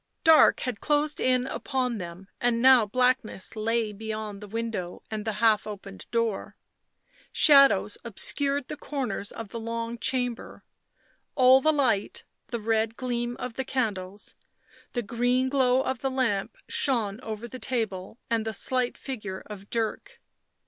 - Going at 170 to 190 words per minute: No, average, 150 wpm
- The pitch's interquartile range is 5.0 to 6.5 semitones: No, average, 3.3 semitones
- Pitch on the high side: Yes, high, 230 Hz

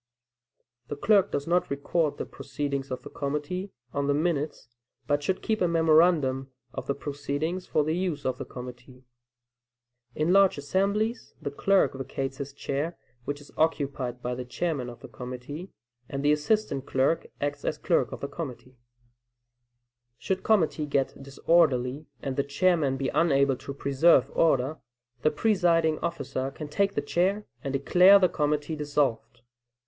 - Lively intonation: No, average, 3.8 semitones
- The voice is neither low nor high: Yes, medium, 145 Hz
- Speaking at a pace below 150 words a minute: No, average, 160 wpm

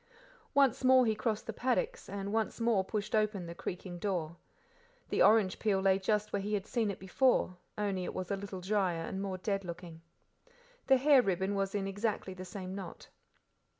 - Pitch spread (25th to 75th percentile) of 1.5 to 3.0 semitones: Yes, narrow, 2.6 semitones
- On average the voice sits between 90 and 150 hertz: No, high, 200 Hz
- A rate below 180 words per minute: No, average, 190 wpm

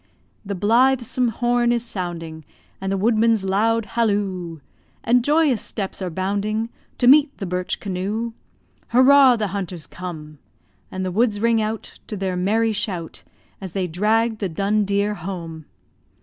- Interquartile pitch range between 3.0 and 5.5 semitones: Yes, average, 3.7 semitones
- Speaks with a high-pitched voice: Yes, high, 205 Hz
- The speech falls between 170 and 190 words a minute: No, average, 150 wpm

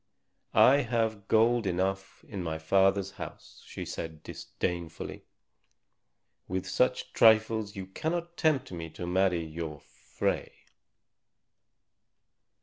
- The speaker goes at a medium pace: No, slow, 105 wpm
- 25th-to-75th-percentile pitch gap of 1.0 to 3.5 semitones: No, average, 4.5 semitones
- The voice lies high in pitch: No, very low, 95 Hz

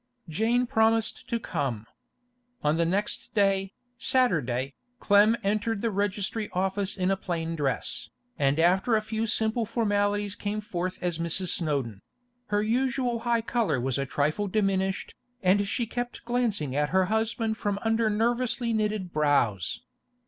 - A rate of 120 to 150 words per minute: Yes, average, 145 wpm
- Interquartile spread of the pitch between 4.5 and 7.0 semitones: Yes, average, 4.9 semitones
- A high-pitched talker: Yes, high, 205 Hz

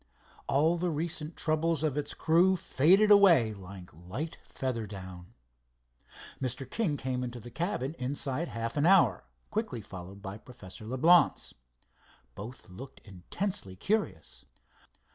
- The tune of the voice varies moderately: No, wide, 7.6 semitones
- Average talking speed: No, slow, 130 wpm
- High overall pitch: No, low, 130 Hz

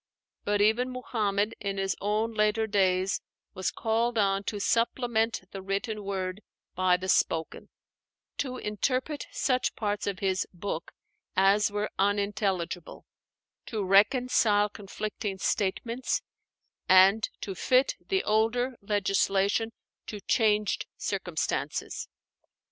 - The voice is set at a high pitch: Yes, high, 205 Hz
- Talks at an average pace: No, slow, 110 wpm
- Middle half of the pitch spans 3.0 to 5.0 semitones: No, narrow, 2.5 semitones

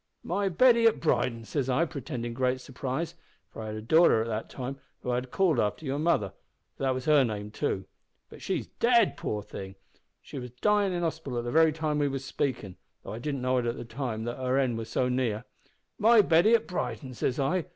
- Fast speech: Yes, fast, 225 wpm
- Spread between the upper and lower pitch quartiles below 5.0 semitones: No, average, 5.3 semitones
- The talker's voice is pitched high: No, low, 130 Hz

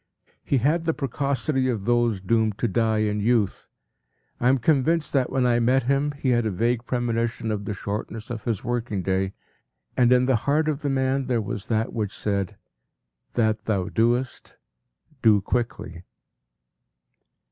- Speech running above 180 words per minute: No, average, 170 wpm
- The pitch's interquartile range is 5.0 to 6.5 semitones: No, average, 3.4 semitones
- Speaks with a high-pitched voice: No, low, 120 Hz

